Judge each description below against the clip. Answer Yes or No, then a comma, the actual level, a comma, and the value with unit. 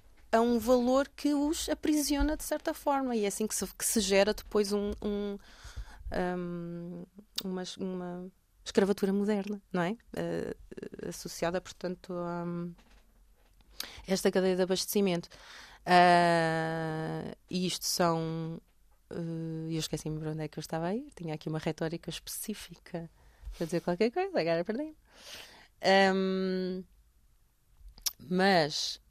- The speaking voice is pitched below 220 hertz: Yes, medium, 185 Hz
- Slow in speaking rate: No, average, 130 wpm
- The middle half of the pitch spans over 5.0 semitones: No, average, 3.8 semitones